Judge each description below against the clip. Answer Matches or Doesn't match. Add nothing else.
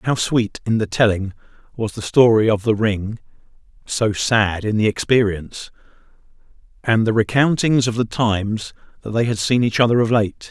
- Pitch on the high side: Doesn't match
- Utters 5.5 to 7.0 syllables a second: Doesn't match